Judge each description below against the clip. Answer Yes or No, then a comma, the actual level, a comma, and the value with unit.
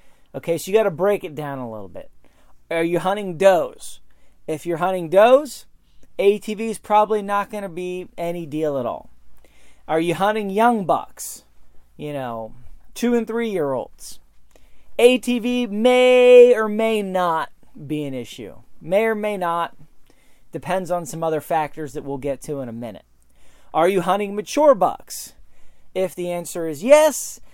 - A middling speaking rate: Yes, average, 165 wpm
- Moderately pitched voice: Yes, medium, 175 Hz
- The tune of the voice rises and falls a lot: Yes, wide, 6.7 semitones